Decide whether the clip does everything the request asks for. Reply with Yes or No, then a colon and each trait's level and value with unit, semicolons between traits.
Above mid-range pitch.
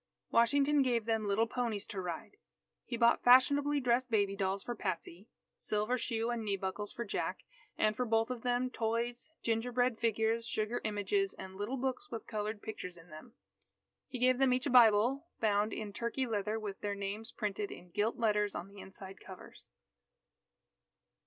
Yes: high, 225 Hz